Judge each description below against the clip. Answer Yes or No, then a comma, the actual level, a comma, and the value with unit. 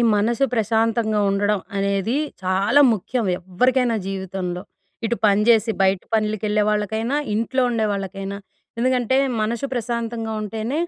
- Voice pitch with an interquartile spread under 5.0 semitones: Yes, average, 2.9 semitones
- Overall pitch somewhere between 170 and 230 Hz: Yes, high, 215 Hz